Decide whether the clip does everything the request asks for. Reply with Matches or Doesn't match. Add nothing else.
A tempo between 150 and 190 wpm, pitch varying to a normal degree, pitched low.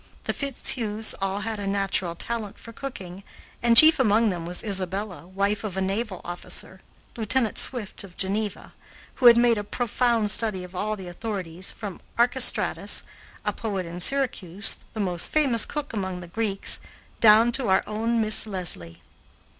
Doesn't match